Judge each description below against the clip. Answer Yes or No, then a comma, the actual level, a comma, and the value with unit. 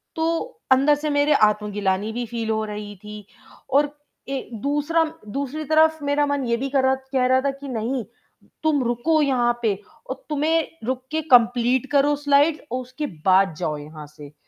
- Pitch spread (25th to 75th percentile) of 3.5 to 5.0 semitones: Yes, average, 4.7 semitones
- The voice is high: Yes, very high, 260 Hz